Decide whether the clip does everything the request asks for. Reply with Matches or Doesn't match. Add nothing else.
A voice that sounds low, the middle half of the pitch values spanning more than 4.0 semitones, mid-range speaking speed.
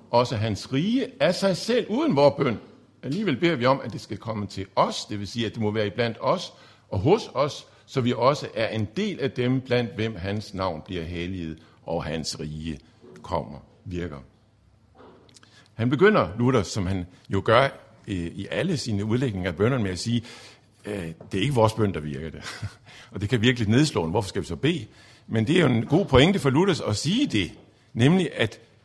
Matches